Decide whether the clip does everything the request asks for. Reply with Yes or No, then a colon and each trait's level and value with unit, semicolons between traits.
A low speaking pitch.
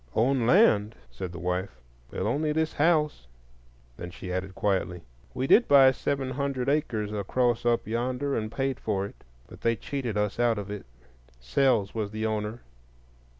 Yes: low, 115 Hz